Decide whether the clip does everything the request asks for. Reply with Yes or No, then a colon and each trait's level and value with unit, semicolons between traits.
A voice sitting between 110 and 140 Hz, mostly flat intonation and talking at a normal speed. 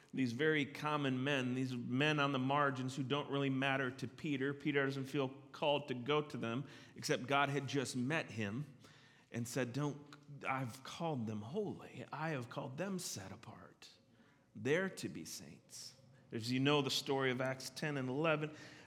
Yes: low, 135 Hz; narrow, 2.2 semitones; average, 180 wpm